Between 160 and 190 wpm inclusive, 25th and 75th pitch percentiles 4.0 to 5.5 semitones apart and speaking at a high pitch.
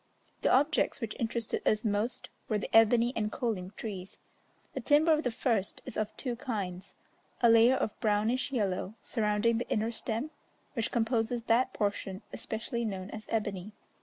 No: average, 165 wpm; narrow, 2.4 semitones; high, 225 Hz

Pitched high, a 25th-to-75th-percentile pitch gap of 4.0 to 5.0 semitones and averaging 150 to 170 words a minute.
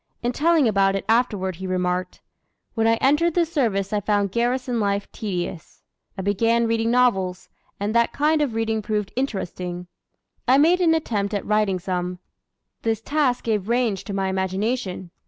Yes: high, 215 Hz; average, 4.3 semitones; average, 165 wpm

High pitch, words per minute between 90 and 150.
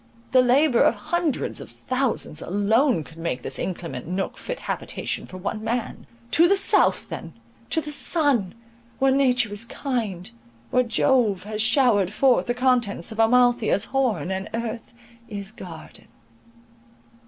Yes: high, 230 Hz; average, 140 wpm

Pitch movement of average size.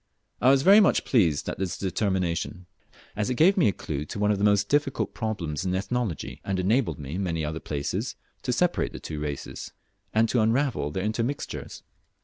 No: wide, 6.3 semitones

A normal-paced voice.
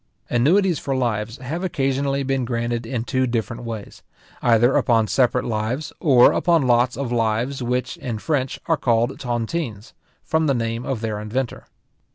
Yes: average, 160 wpm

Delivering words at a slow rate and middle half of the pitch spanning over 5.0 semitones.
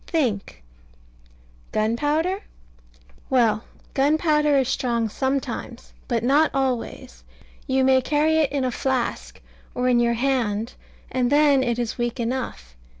No: slow, 125 wpm; average, 3.2 semitones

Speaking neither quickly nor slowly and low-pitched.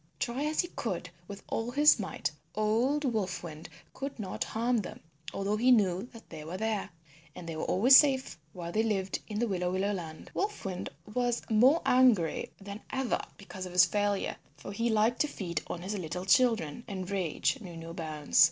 No: average, 195 wpm; high, 205 Hz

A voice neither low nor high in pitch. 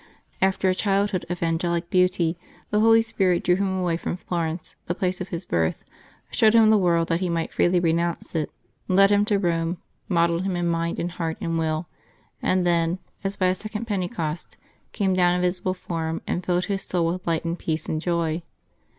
Yes: medium, 175 Hz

